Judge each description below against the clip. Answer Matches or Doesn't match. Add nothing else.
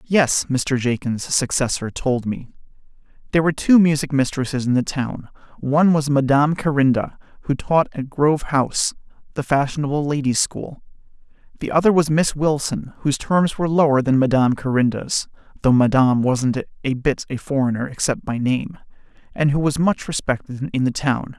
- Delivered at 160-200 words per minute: Doesn't match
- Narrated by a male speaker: Matches